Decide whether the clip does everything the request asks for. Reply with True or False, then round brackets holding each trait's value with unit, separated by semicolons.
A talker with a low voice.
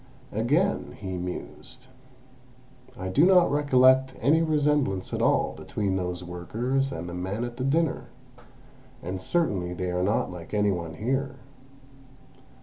True (115 Hz)